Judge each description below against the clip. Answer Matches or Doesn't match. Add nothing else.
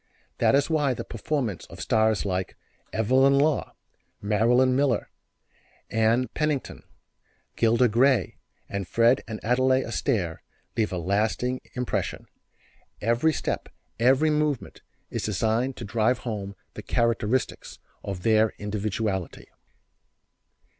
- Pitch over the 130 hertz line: Doesn't match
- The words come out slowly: Matches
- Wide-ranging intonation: Doesn't match